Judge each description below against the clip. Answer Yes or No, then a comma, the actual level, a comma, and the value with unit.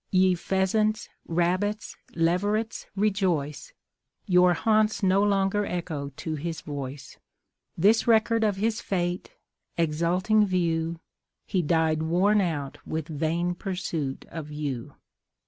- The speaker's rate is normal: No, slow, 110 wpm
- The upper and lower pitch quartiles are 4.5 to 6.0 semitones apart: No, average, 4.1 semitones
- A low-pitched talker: No, medium, 180 Hz